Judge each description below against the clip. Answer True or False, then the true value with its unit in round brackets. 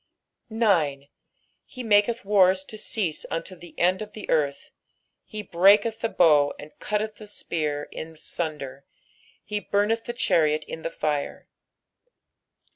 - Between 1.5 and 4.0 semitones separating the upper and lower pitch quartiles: False (5.5 semitones)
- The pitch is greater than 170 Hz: True (185 Hz)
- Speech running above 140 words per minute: False (135 wpm)